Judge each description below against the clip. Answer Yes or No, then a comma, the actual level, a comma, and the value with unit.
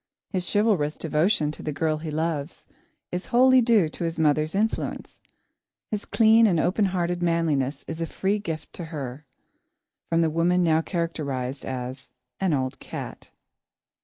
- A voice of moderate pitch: Yes, medium, 165 Hz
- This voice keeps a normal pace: Yes, average, 155 wpm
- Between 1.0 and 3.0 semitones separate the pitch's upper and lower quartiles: No, average, 3.5 semitones